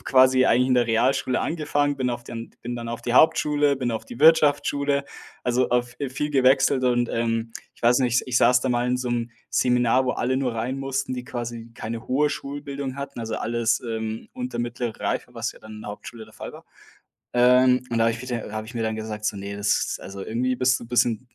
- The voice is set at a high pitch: No, low, 125 Hz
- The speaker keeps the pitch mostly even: Yes, narrow, 2.2 semitones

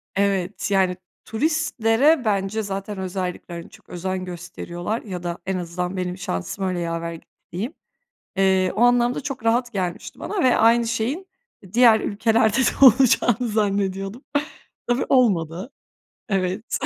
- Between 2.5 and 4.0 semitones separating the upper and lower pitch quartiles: No, average, 4.4 semitones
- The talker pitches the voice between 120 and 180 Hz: No, high, 200 Hz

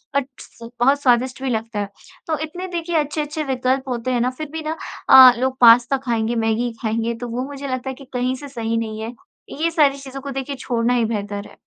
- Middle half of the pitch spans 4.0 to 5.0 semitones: No, average, 3.2 semitones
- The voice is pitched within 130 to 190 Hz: No, very high, 255 Hz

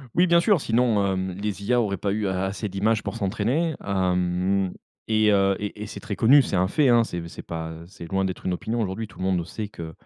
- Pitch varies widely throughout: No, average, 3.2 semitones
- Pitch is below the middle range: Yes, low, 100 Hz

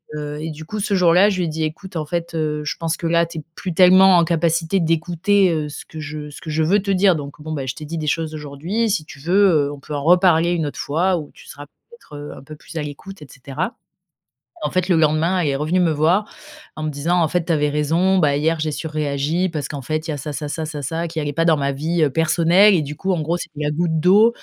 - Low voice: No, medium, 160 Hz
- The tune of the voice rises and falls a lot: No, average, 2.9 semitones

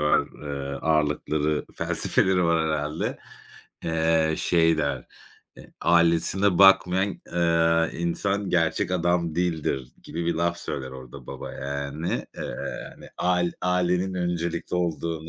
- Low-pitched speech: Yes, very low, 85 Hz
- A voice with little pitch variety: Yes, narrow, 2.3 semitones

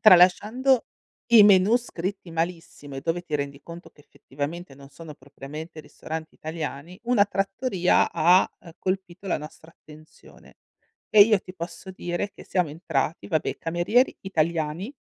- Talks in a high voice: No, medium, 170 Hz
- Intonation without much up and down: No, average, 3.7 semitones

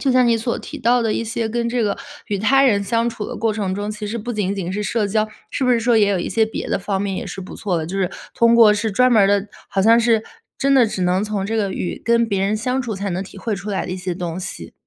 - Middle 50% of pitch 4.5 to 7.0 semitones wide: No, average, 3.0 semitones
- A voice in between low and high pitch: No, high, 210 Hz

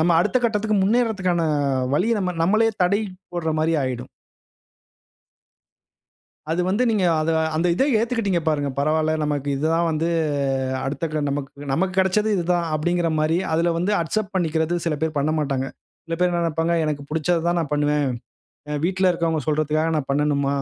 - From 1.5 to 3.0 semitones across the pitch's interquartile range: No, average, 3.5 semitones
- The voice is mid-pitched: Yes, medium, 165 Hz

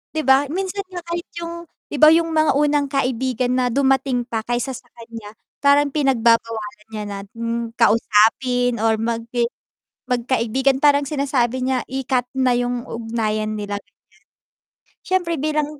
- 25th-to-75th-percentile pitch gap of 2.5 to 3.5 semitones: No, average, 3.9 semitones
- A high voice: Yes, very high, 255 Hz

